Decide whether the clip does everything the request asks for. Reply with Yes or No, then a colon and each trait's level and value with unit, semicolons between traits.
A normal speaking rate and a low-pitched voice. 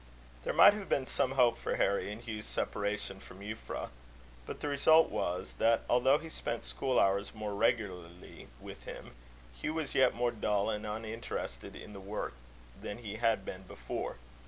Yes: average, 175 wpm; low, 110 Hz